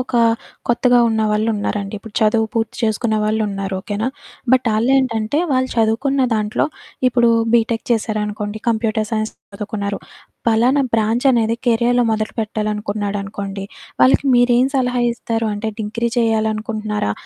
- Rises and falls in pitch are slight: Yes, narrow, 2.0 semitones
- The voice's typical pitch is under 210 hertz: No, high, 220 Hz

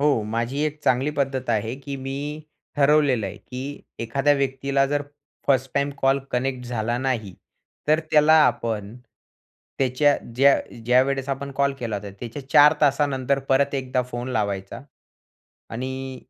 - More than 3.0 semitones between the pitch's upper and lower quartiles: No, narrow, 2.5 semitones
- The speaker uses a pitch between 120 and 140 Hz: Yes, low, 135 Hz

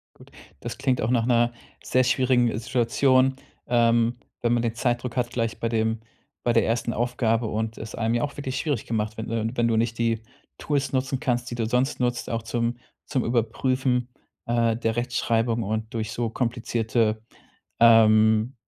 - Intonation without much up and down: Yes, narrow, 1.5 semitones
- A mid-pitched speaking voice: No, low, 115 Hz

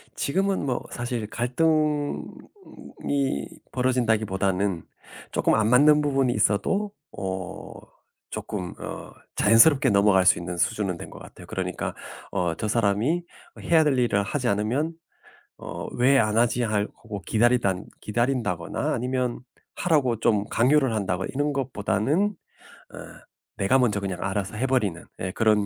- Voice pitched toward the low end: Yes, low, 115 Hz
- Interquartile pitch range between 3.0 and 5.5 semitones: Yes, average, 5.1 semitones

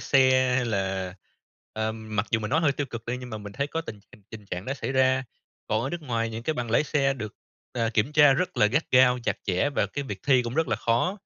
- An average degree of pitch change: Yes, average, 4.0 semitones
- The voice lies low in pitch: Yes, low, 125 Hz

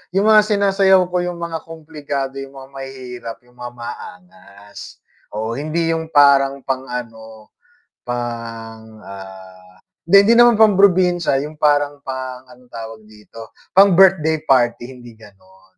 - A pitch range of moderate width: No, wide, 6.6 semitones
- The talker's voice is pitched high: No, low, 135 Hz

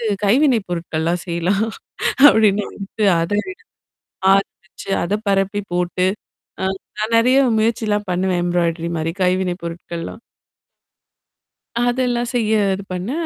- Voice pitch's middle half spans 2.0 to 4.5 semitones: Yes, average, 3.9 semitones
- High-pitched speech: Yes, high, 195 Hz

